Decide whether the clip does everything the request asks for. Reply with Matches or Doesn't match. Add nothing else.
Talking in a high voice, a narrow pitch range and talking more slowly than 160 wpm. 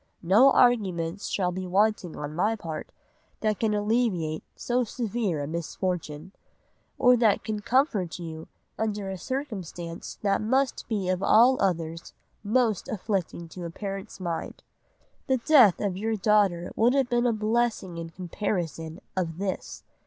Doesn't match